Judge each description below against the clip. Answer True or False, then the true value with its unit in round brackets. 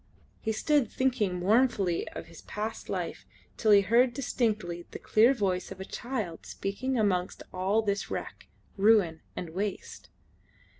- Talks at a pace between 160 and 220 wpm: False (145 wpm)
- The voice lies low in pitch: False (210 Hz)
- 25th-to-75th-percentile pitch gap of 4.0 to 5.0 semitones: True (4.3 semitones)